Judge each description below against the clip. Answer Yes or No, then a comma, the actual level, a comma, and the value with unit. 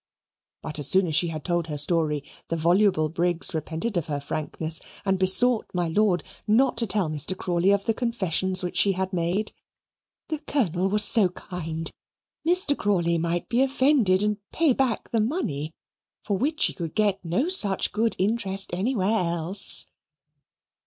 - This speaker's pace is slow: No, average, 165 wpm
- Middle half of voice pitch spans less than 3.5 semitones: No, average, 4.5 semitones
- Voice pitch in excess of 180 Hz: Yes, high, 190 Hz